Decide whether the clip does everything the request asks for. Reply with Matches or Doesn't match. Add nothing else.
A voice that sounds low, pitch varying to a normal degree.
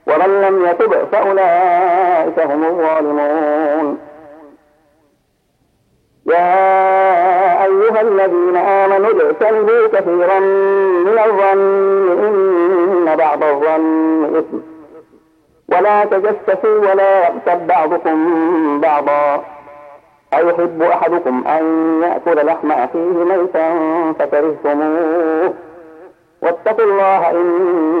Doesn't match